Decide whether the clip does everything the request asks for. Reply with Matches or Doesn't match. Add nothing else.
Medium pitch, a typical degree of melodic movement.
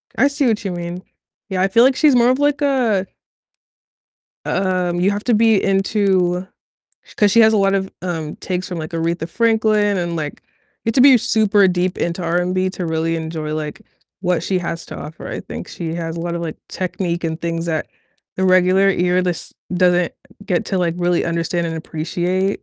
Matches